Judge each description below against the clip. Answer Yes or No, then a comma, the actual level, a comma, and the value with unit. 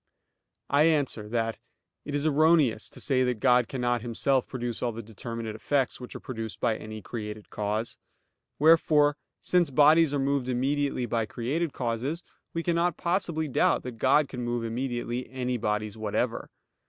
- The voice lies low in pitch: Yes, low, 125 Hz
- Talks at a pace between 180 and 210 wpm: No, average, 160 wpm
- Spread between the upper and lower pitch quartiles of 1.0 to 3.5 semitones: No, average, 4.1 semitones